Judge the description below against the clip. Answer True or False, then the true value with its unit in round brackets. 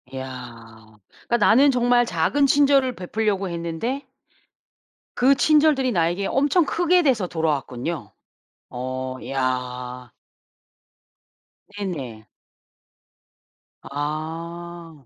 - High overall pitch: False (170 Hz)